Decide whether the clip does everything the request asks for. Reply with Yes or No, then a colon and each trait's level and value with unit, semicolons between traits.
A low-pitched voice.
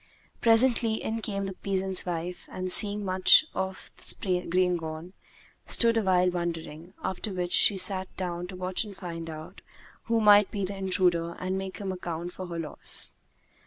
No: medium, 185 Hz